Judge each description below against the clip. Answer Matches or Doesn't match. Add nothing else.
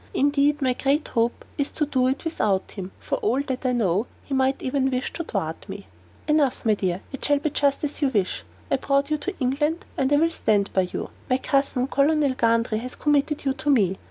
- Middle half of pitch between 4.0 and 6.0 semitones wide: Doesn't match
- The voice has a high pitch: Matches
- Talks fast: Matches